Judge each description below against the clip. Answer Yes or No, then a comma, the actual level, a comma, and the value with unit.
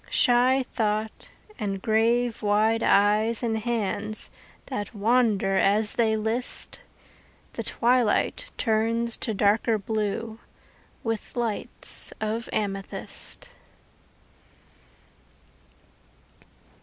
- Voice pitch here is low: No, high, 220 Hz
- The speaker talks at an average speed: No, slow, 80 wpm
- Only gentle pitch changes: Yes, narrow, 1.9 semitones